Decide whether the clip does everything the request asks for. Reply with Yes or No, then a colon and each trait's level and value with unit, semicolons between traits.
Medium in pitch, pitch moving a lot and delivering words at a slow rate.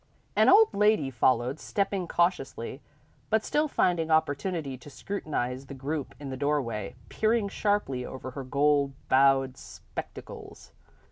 Yes: medium, 145 Hz; wide, 6.2 semitones; slow, 130 wpm